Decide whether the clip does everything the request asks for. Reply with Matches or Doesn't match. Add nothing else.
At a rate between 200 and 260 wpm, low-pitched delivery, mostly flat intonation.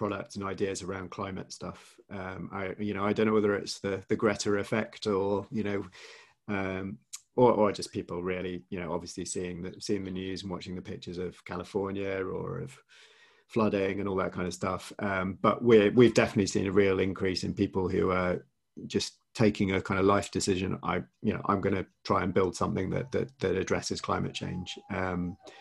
Matches